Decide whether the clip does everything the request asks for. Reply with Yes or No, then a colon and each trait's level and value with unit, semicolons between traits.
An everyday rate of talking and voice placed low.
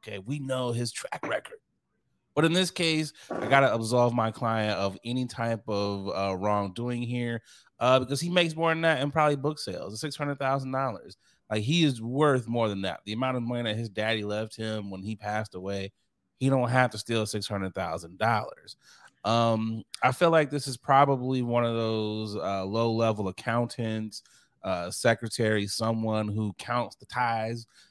Yes: average, 175 wpm; low, 115 Hz